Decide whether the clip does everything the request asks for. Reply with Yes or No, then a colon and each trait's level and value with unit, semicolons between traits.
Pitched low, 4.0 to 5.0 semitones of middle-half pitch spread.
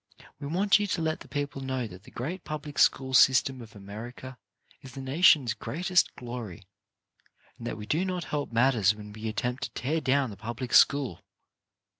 Yes: low, 130 Hz; average, 4.3 semitones